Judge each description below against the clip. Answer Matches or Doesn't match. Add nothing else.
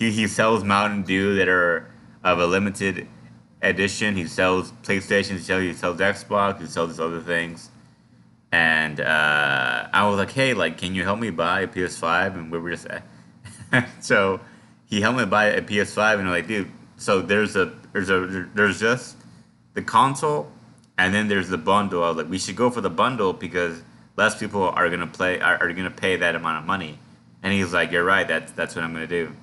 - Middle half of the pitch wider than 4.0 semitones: Doesn't match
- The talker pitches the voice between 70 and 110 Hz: Matches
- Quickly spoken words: Matches